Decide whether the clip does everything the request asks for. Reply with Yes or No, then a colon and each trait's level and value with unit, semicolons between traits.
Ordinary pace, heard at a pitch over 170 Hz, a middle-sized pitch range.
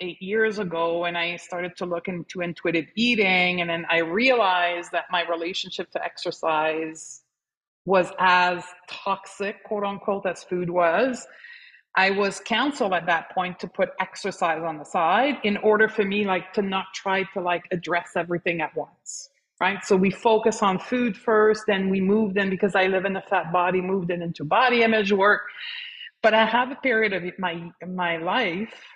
Yes: average, 180 wpm; high, 190 Hz; average, 3.2 semitones